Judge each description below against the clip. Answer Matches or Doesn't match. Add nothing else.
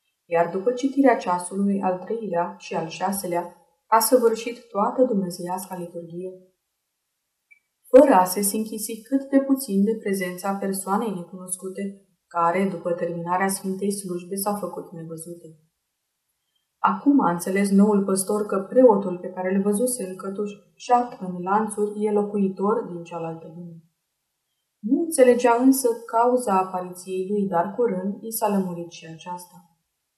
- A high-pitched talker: Matches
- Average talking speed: Matches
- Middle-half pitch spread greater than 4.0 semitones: Doesn't match